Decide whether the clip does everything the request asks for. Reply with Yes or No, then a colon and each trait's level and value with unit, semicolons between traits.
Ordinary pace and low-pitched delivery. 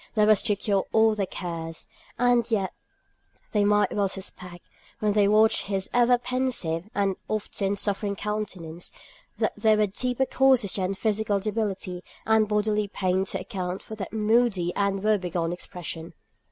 No: average, 155 wpm; high, 205 Hz